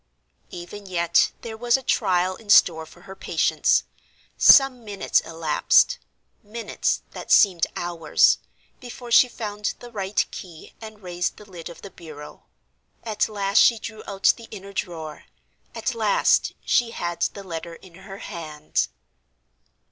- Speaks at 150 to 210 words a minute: No, average, 140 wpm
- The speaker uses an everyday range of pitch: Yes, average, 4.2 semitones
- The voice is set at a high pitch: Yes, high, 195 Hz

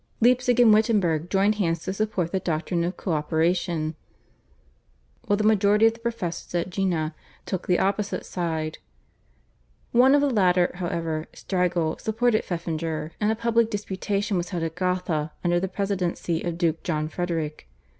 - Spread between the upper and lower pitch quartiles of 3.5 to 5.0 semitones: Yes, average, 4.0 semitones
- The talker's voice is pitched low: No, medium, 180 Hz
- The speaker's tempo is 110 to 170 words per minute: Yes, average, 155 wpm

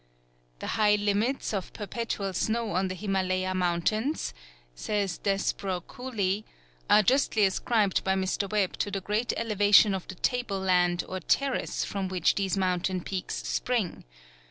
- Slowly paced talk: No, average, 145 wpm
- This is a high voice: Yes, high, 195 Hz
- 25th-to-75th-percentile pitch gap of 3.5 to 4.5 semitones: No, narrow, 2.4 semitones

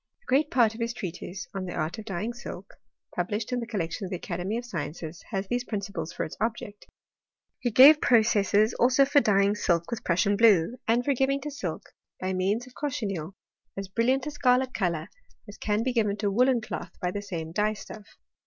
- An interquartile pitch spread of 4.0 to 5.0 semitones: Yes, average, 4.6 semitones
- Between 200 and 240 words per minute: Yes, fast, 205 wpm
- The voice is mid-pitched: No, high, 210 Hz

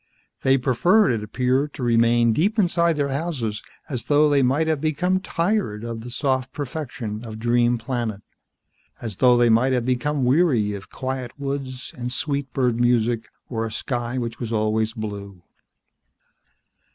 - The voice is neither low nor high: No, low, 125 Hz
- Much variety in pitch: No, average, 3.6 semitones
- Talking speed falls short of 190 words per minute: Yes, average, 160 wpm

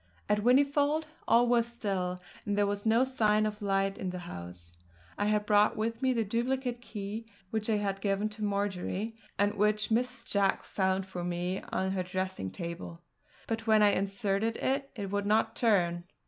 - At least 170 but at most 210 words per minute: Yes, average, 180 wpm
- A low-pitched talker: No, high, 205 Hz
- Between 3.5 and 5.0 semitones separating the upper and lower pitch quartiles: No, average, 3.0 semitones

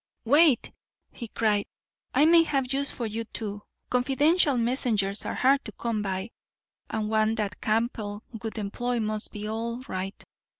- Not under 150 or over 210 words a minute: Yes, average, 155 wpm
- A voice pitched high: Yes, high, 225 Hz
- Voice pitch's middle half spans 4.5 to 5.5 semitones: No, average, 3.2 semitones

